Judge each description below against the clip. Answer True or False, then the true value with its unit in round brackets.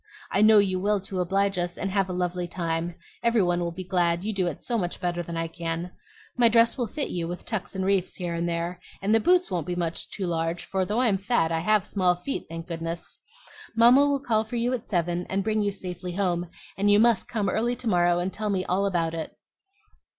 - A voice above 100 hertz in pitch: True (185 Hz)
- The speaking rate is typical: False (240 wpm)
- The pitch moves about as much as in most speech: True (3.5 semitones)